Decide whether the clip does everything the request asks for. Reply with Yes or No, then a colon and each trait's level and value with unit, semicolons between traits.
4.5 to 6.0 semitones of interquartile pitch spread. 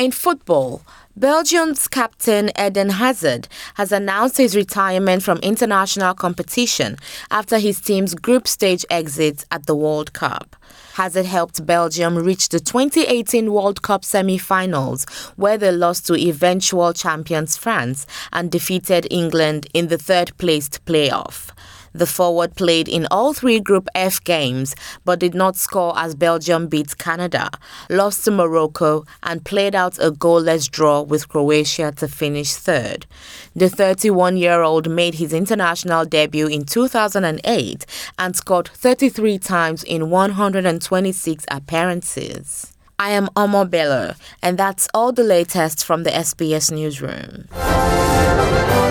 No: average, 3.7 semitones